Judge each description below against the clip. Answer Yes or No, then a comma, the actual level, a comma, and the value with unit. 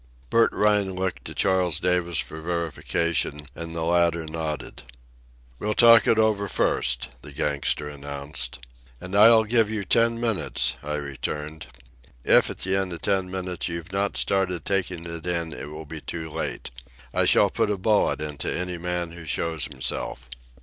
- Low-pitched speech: Yes, very low, 85 Hz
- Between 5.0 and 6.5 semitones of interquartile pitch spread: No, average, 4.1 semitones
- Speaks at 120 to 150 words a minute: No, average, 165 wpm